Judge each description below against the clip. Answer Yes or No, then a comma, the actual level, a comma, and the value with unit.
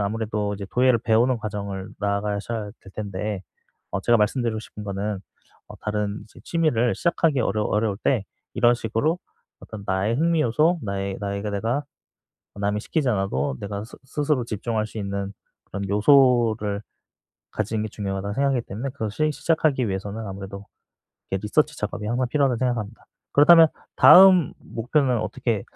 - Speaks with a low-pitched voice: Yes, low, 110 Hz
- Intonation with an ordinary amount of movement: Yes, average, 4.0 semitones